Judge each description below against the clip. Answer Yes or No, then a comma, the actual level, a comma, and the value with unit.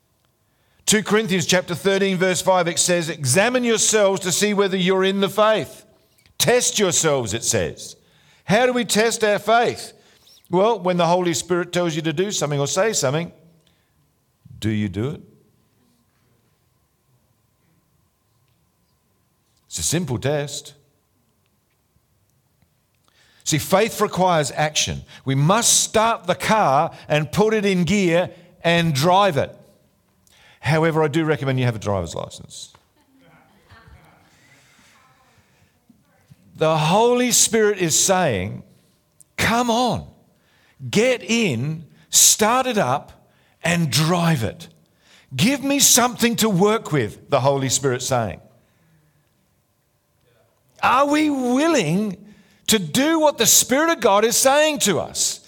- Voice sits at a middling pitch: Yes, medium, 175 Hz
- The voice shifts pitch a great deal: Yes, wide, 7.0 semitones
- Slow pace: Yes, slow, 120 wpm